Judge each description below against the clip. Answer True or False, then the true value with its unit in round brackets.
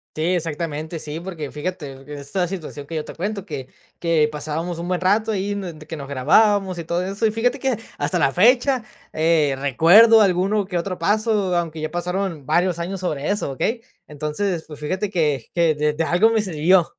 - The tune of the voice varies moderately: True (4.5 semitones)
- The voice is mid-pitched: True (175 Hz)